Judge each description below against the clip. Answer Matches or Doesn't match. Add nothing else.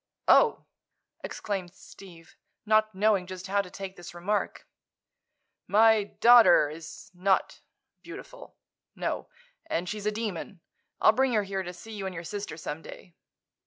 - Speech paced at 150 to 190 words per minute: Doesn't match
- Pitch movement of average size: Matches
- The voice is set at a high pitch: Matches